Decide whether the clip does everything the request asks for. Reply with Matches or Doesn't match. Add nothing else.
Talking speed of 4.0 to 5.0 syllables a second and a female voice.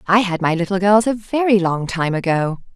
Doesn't match